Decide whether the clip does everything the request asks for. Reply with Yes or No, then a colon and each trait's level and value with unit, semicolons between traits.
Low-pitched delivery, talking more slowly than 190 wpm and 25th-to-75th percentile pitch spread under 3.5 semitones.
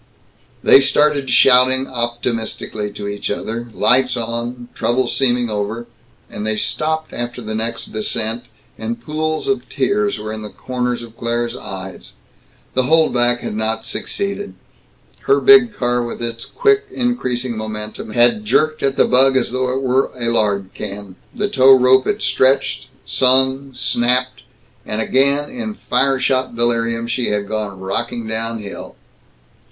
Yes: low, 120 Hz; average, 150 wpm; average, 3.0 semitones